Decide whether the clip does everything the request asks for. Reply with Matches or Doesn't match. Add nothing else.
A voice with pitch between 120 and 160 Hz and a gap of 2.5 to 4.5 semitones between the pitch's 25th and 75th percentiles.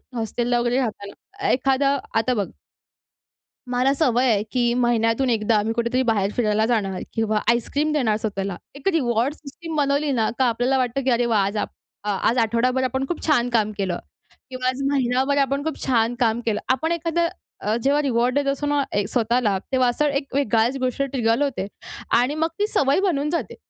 Doesn't match